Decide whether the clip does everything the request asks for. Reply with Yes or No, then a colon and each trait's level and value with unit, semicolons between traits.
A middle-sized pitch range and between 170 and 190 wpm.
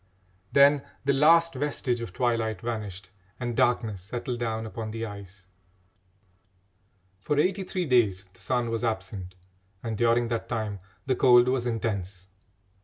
No: average, 3.5 semitones; average, 140 wpm